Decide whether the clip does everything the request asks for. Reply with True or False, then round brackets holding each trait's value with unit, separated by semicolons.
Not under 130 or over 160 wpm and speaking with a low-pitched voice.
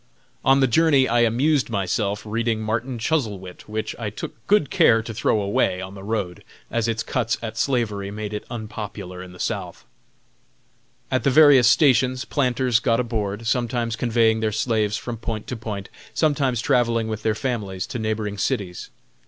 False (170 wpm; 115 Hz)